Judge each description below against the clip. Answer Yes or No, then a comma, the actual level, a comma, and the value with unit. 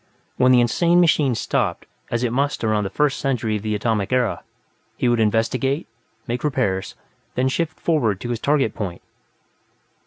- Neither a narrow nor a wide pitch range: Yes, average, 4.1 semitones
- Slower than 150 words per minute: No, average, 165 wpm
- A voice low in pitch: Yes, low, 120 Hz